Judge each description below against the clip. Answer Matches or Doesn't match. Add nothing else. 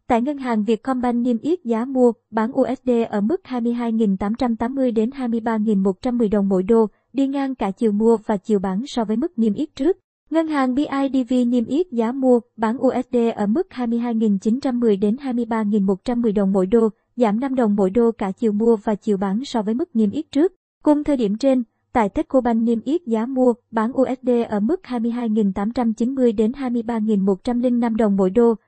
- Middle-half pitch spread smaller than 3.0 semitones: Matches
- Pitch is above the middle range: Matches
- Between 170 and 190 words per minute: Matches